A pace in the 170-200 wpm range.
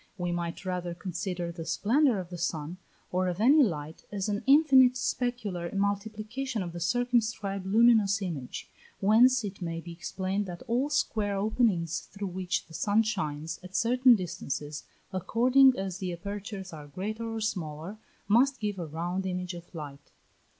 No: average, 160 wpm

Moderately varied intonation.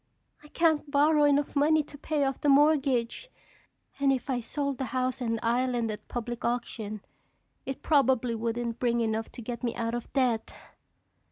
Yes: average, 3.5 semitones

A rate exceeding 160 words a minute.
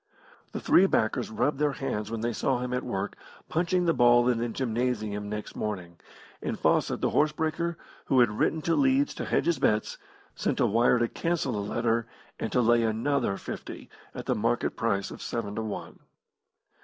Yes: average, 190 wpm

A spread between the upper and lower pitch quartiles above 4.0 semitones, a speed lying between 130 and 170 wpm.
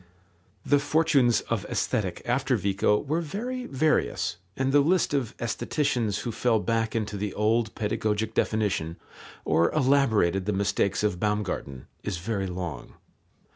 Yes: wide, 5.5 semitones; slow, 135 wpm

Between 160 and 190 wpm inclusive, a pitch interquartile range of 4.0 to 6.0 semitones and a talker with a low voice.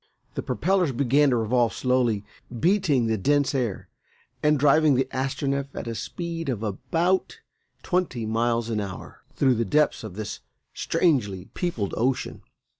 No: average, 145 wpm; average, 4.9 semitones; low, 130 Hz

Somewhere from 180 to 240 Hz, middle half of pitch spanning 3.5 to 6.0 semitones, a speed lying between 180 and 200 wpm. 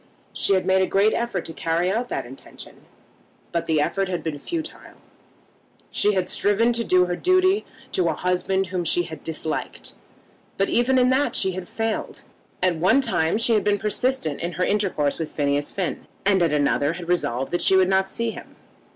Yes: medium, 185 Hz; average, 4.7 semitones; average, 195 wpm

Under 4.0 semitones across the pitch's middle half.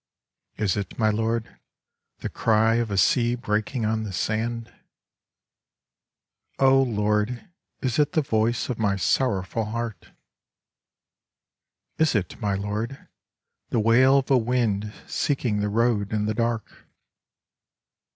Yes: narrow, 2.6 semitones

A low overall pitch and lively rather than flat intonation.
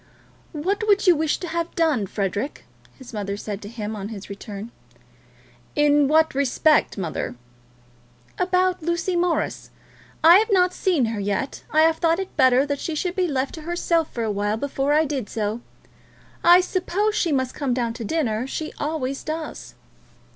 No: very high, 295 Hz; wide, 6.8 semitones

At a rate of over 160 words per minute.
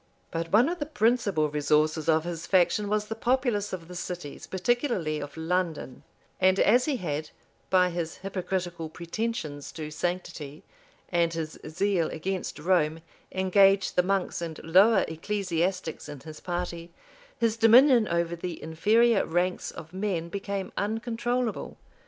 No: average, 140 wpm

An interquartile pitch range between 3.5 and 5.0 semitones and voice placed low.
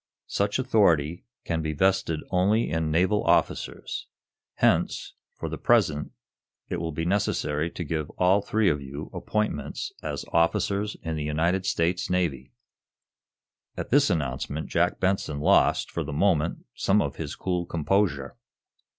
Yes: average, 4.2 semitones; very low, 85 Hz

